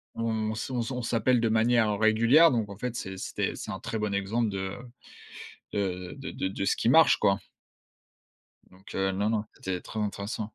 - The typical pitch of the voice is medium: No, low, 110 Hz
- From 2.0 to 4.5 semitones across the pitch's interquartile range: Yes, average, 2.8 semitones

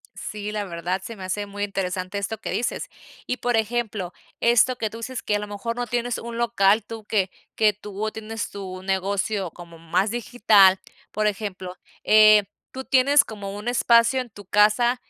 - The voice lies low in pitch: No, high, 210 Hz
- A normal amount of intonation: Yes, average, 3.0 semitones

